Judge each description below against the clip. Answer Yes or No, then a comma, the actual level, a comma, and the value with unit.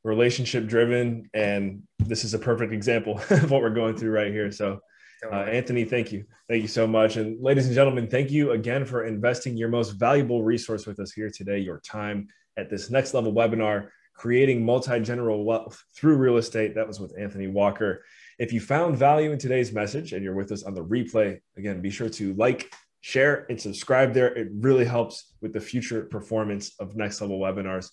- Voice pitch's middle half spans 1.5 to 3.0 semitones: Yes, average, 2.7 semitones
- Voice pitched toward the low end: Yes, low, 110 Hz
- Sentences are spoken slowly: No, average, 200 wpm